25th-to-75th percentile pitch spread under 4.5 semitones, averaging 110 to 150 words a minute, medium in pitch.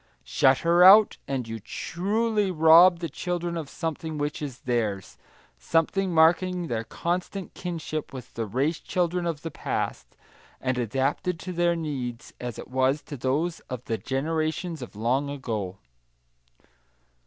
No: average, 5.1 semitones; average, 145 wpm; medium, 155 Hz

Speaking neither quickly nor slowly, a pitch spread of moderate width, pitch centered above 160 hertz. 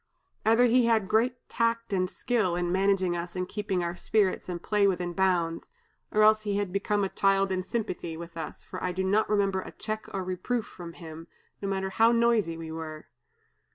Yes: average, 195 wpm; average, 3.4 semitones; high, 190 Hz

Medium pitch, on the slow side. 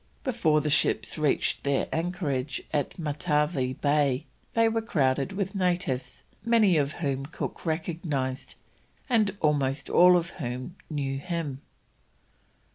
Yes: medium, 150 Hz; slow, 120 wpm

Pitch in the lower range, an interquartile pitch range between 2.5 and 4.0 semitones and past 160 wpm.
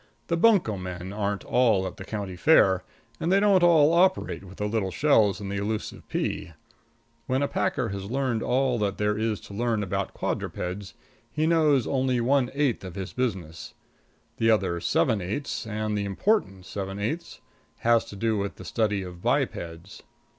No: low, 105 Hz; wide, 5.4 semitones; average, 175 wpm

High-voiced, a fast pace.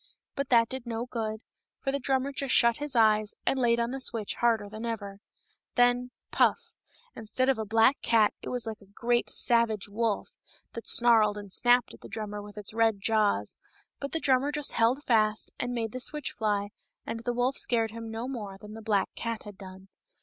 Yes: high, 230 Hz; fast, 210 wpm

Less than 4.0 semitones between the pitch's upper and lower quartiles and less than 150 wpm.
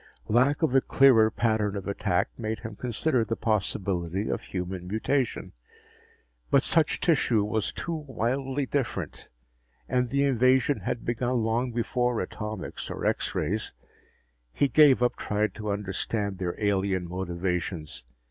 No: average, 4.4 semitones; average, 140 wpm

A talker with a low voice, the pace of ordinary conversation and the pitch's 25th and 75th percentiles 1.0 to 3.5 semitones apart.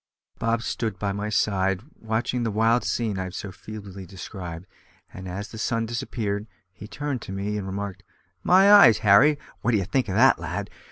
Yes: low, 105 Hz; average, 185 wpm; average, 3.1 semitones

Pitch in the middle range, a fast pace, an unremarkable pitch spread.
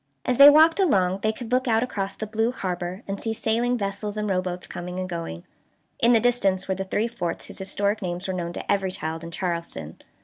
No: high, 195 Hz; fast, 225 wpm; average, 3.9 semitones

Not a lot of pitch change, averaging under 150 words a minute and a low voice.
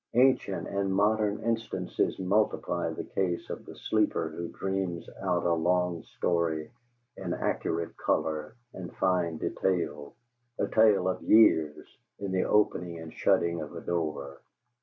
No: average, 3.1 semitones; average, 140 wpm; very low, 90 Hz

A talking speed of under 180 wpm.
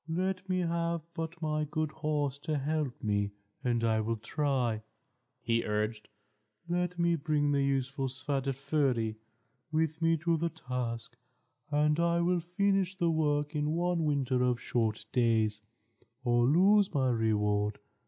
Yes: average, 145 wpm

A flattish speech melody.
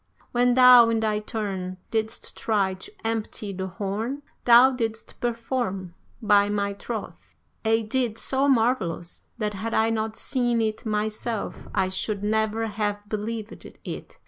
Yes: narrow, 2.1 semitones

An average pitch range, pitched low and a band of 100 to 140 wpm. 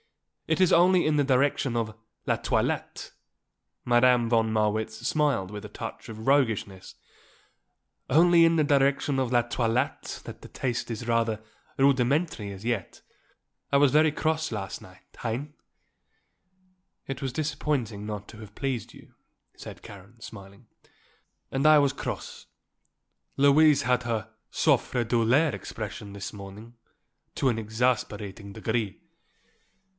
Yes: average, 4.4 semitones; low, 120 Hz; slow, 135 wpm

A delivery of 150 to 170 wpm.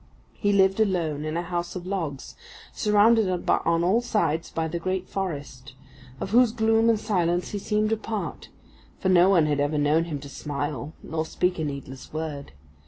No: average, 180 wpm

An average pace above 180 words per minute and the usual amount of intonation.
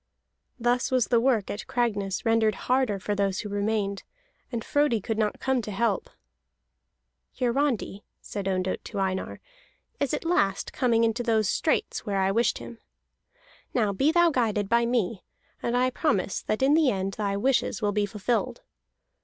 No: average, 165 wpm; average, 3.6 semitones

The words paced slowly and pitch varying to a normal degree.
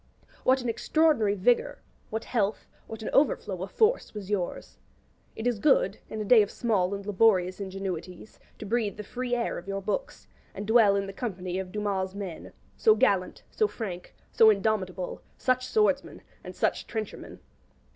No: average, 170 wpm; average, 3.8 semitones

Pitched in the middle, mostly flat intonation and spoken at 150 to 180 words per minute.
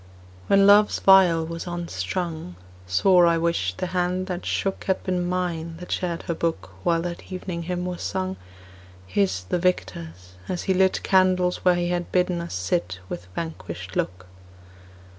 Yes: medium, 175 Hz; narrow, 2.3 semitones; average, 160 wpm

